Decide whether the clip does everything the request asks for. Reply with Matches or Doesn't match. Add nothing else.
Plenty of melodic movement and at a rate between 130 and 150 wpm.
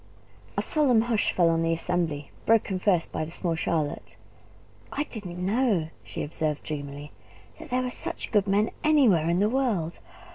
Doesn't match